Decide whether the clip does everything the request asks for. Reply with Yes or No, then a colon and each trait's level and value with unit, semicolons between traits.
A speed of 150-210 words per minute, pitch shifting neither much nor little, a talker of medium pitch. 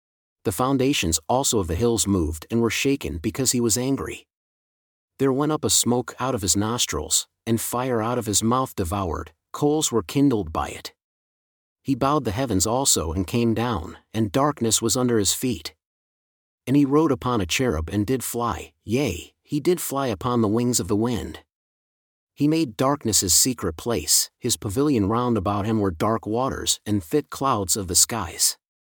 No: average, 180 wpm; average, 4.7 semitones; low, 115 Hz